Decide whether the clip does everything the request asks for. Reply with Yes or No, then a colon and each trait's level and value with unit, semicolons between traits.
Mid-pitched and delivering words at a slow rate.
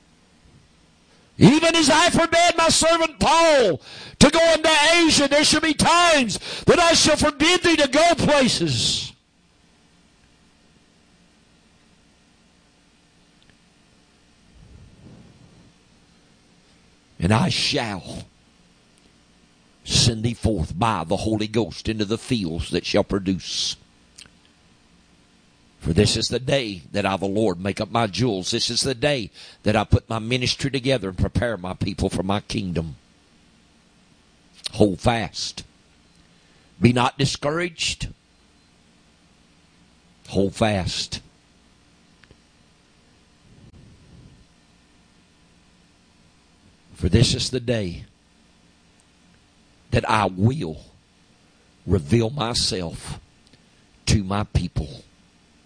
No: low, 105 Hz; slow, 95 wpm